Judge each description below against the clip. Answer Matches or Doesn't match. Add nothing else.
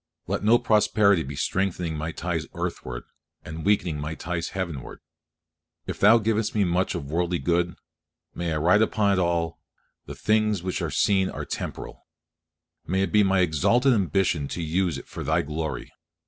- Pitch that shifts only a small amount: Doesn't match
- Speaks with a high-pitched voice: Doesn't match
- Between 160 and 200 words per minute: Matches